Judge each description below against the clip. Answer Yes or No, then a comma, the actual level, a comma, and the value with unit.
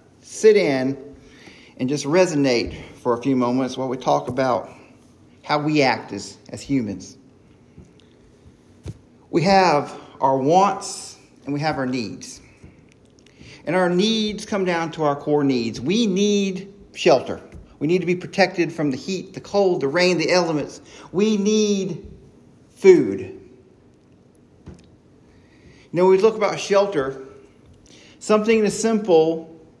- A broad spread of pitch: Yes, wide, 6.0 semitones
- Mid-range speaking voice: Yes, medium, 165 Hz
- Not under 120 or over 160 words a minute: Yes, slow, 135 wpm